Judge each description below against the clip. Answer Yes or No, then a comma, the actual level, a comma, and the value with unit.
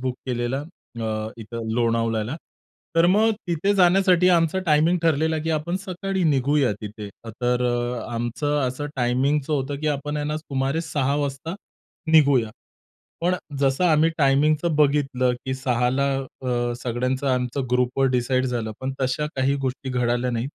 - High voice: No, low, 135 Hz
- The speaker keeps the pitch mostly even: No, average, 3.8 semitones